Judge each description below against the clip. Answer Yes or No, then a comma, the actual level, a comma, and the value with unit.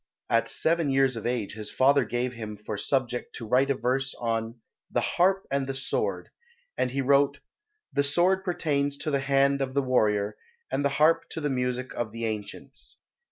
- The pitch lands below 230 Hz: Yes, low, 135 Hz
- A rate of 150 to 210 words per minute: Yes, average, 190 wpm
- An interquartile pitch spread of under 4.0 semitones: Yes, average, 3.3 semitones